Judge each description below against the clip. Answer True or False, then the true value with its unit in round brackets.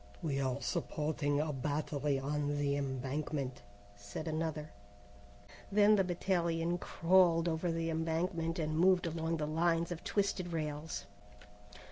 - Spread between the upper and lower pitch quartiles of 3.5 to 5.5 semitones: False (2.6 semitones)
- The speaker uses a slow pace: True (125 wpm)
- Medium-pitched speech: True (160 Hz)